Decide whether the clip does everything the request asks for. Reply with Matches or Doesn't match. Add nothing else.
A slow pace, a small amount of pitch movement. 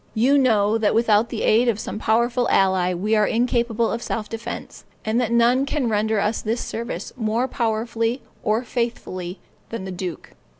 Doesn't match